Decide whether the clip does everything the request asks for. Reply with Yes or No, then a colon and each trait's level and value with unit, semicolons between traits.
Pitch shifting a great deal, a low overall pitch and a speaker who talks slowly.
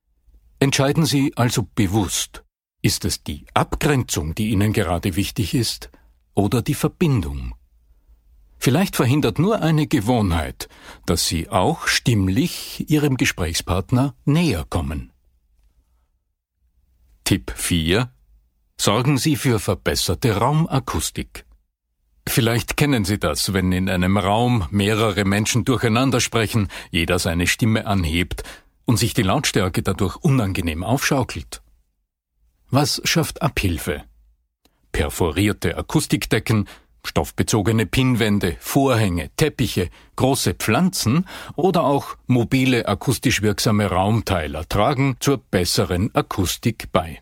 Yes: wide, 7.4 semitones; low, 105 Hz; slow, 105 wpm